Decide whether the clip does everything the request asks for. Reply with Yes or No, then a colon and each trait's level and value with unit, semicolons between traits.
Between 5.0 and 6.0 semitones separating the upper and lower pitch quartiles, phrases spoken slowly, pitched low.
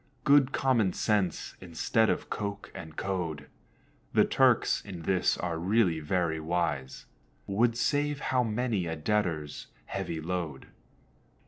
Yes: wide, 5.4 semitones; slow, 125 wpm; very low, 95 Hz